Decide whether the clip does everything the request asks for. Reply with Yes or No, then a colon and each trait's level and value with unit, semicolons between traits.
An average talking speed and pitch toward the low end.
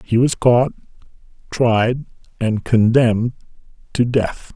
No: slow, 105 wpm; low, 115 Hz